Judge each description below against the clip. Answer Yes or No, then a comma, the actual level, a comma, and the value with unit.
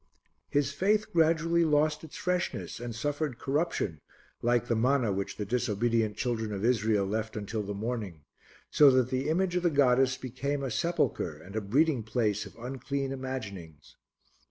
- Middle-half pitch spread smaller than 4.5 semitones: No, average, 5.2 semitones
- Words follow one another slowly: No, average, 160 wpm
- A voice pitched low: Yes, low, 125 Hz